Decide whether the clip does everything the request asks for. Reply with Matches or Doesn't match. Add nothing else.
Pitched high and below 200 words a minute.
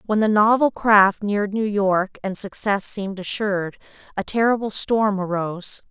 Matches